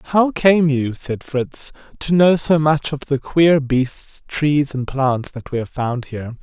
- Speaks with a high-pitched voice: No, medium, 145 Hz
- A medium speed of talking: Yes, average, 195 wpm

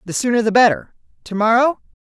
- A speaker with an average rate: Yes, average, 145 wpm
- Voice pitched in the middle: No, high, 230 Hz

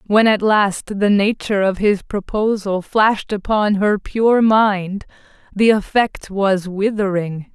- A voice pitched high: Yes, high, 205 Hz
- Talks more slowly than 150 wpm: Yes, slow, 135 wpm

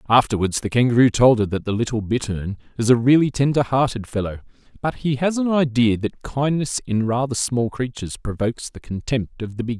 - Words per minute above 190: Yes, average, 200 wpm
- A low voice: Yes, low, 120 Hz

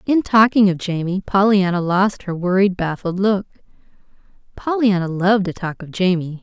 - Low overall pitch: No, high, 190 Hz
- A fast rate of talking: No, average, 150 wpm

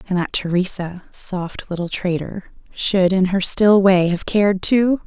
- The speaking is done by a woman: Yes, female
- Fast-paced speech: No, average, 165 wpm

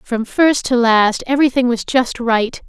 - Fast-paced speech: No, average, 180 wpm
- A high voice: Yes, high, 245 Hz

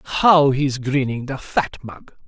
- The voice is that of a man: Yes, male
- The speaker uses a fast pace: No, average, 160 wpm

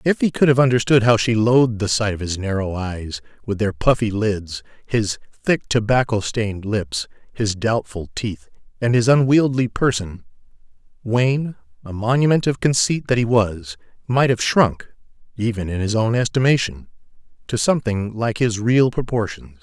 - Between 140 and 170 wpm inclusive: Yes, average, 160 wpm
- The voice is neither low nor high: No, low, 115 Hz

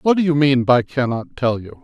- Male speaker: Yes, male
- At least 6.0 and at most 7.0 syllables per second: No, 5.1 syllables/s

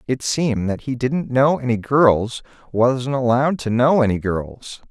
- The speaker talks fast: No, average, 160 wpm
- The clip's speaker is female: No, male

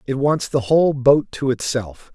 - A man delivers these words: Yes, male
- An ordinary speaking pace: Yes, average, 195 wpm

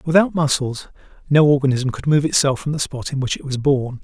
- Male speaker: Yes, male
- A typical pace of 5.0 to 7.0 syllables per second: Yes, 5.7 syllables/s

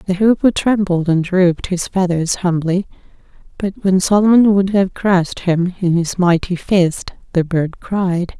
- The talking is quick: No, average, 155 wpm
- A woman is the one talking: Yes, female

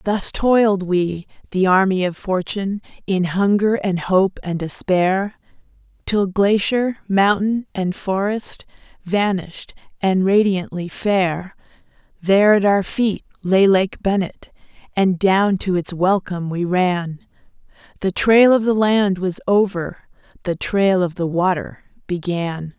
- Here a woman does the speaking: Yes, female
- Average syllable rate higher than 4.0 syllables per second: No, 3.8 syllables/s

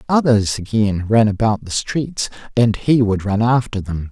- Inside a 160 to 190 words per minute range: Yes, average, 175 wpm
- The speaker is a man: Yes, male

